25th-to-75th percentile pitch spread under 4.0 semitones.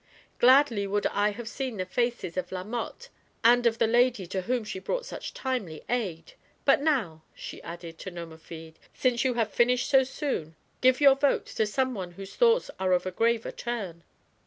No: wide, 5.6 semitones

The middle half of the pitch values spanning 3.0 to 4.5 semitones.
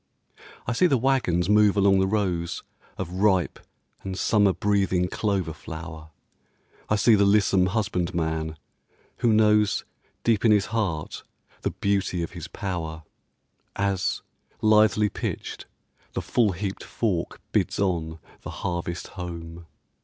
Yes: average, 3.5 semitones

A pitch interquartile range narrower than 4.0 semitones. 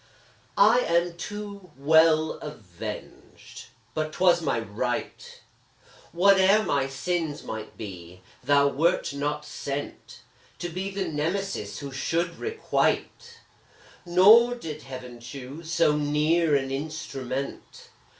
No: average, 4.6 semitones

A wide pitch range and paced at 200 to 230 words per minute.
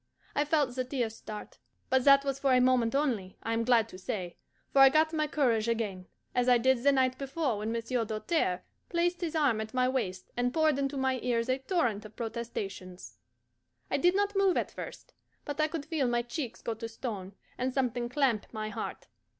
No: average, 3.8 semitones; fast, 205 wpm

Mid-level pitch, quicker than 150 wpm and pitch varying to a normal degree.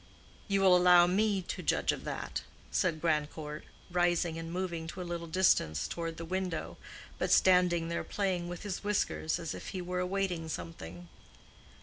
No: medium, 175 Hz; average, 165 wpm; narrow, 2.1 semitones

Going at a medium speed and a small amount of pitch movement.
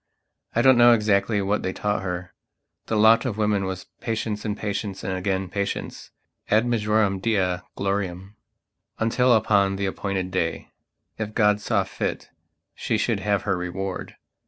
Yes: average, 145 wpm; narrow, 2.2 semitones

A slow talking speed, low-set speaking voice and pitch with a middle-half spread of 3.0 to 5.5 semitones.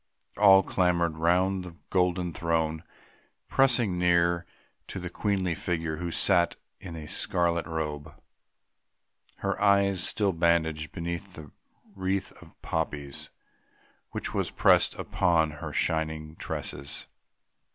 No: slow, 120 wpm; very low, 85 Hz; narrow, 2.5 semitones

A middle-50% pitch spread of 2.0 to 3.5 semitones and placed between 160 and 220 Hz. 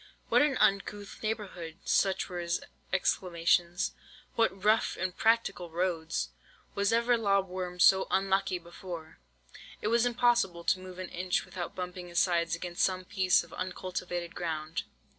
Yes: narrow, 2.4 semitones; medium, 185 Hz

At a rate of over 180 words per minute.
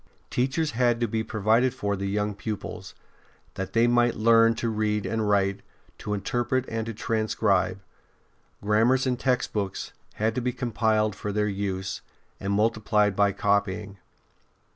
No: average, 145 wpm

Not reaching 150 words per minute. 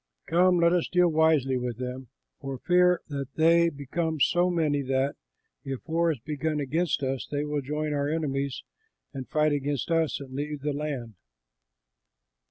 No: average, 165 wpm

